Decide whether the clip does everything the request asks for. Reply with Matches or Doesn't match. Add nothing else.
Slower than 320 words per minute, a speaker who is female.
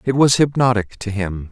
Doesn't match